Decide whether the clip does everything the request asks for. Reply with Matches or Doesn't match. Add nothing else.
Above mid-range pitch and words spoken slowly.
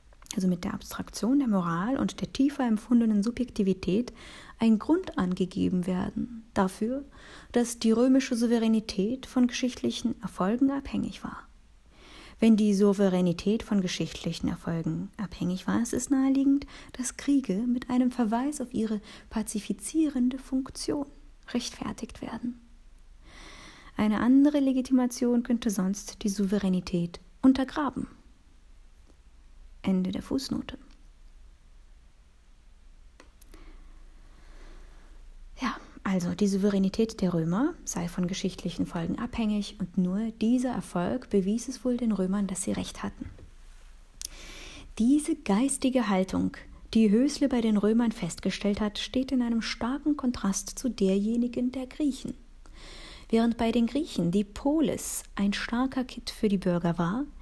Matches